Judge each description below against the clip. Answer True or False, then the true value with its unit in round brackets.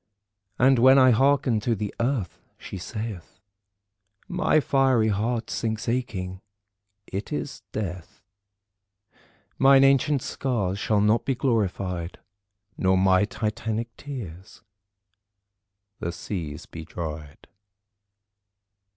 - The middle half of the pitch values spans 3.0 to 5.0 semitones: False (5.6 semitones)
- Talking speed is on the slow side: True (100 wpm)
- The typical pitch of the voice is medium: False (110 Hz)